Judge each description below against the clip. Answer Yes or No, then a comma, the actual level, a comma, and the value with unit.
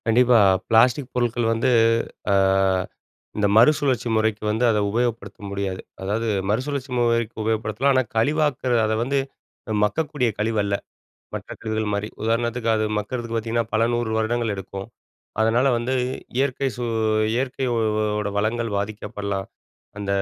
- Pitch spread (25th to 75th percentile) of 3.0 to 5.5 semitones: No, narrow, 2.5 semitones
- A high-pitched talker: No, low, 115 Hz